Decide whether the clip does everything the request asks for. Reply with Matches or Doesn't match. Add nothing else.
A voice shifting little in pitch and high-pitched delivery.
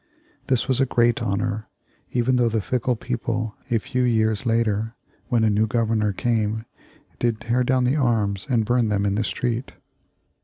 Doesn't match